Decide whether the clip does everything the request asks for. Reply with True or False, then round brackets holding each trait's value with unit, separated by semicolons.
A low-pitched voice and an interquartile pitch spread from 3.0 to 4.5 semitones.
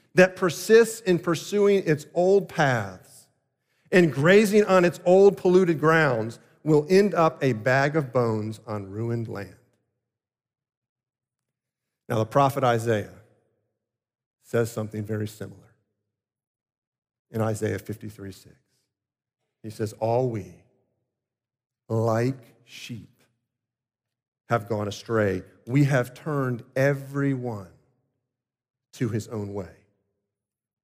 True (125 Hz; 4.1 semitones)